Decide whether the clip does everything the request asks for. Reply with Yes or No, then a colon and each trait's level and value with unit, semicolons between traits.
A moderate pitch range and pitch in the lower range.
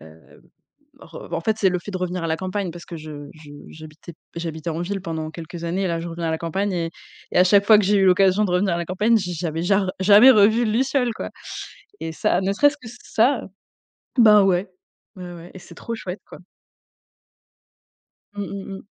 No: average, 3.4 semitones; medium, 185 Hz